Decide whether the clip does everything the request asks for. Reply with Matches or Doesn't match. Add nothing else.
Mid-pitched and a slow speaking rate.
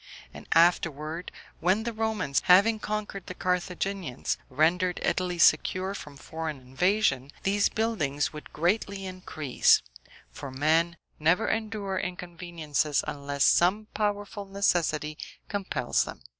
Matches